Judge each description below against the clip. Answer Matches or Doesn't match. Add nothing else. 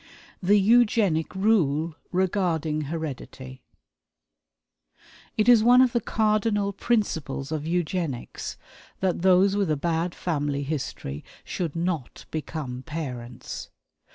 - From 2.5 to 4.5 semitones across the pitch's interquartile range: Doesn't match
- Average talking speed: Doesn't match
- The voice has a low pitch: Doesn't match